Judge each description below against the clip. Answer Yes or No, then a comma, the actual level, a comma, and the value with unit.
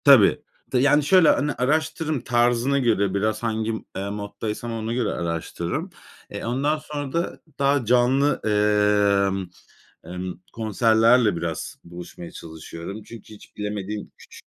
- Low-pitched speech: Yes, low, 110 Hz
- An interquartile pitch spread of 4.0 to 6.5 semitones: Yes, average, 4.7 semitones